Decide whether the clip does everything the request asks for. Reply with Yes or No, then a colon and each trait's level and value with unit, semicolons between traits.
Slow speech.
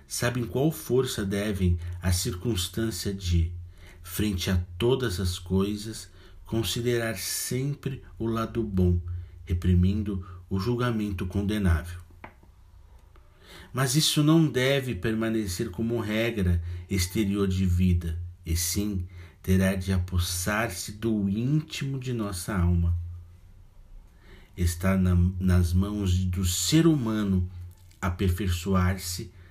Yes: slow, 100 wpm